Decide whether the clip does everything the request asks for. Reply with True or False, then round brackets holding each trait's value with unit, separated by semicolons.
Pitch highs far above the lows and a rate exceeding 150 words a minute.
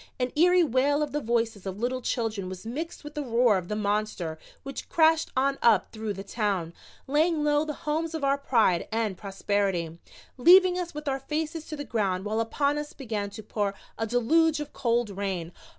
True (6.5 semitones; 200 wpm)